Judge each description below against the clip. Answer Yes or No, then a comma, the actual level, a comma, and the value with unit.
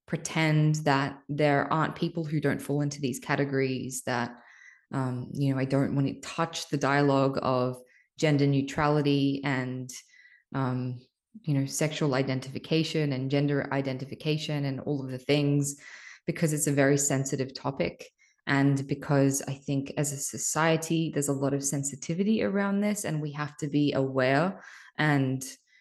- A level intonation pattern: Yes, narrow, 2.2 semitones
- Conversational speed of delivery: Yes, average, 155 wpm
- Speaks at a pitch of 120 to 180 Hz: Yes, medium, 140 Hz